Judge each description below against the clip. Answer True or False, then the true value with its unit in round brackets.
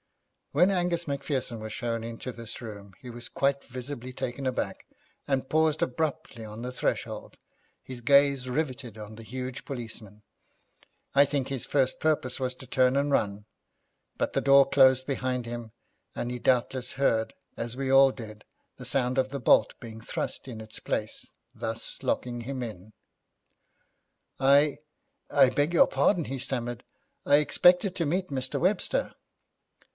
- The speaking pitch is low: True (130 Hz)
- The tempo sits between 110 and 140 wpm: False (155 wpm)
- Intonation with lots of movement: False (3.0 semitones)